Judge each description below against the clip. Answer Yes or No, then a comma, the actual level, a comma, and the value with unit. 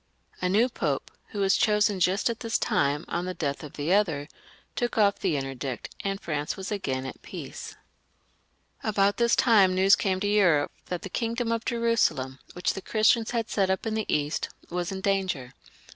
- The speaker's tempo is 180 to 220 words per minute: Yes, average, 190 wpm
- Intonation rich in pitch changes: Yes, wide, 6.0 semitones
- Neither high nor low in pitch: No, high, 195 Hz